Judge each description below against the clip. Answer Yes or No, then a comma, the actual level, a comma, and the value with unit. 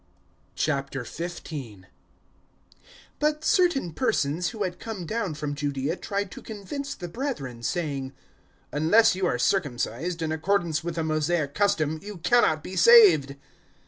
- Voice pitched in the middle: Yes, medium, 170 Hz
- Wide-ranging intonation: Yes, wide, 5.8 semitones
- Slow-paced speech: Yes, slow, 130 wpm